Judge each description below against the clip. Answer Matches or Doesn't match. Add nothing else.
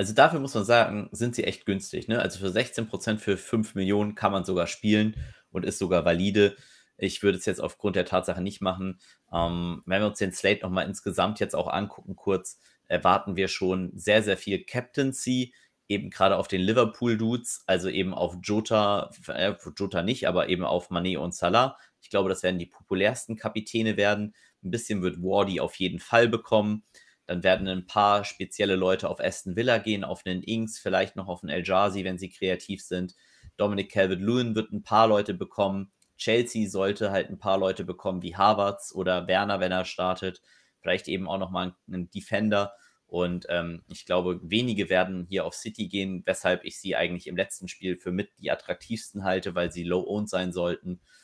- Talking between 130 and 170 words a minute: Doesn't match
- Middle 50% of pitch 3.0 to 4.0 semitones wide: Doesn't match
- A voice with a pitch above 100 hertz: Doesn't match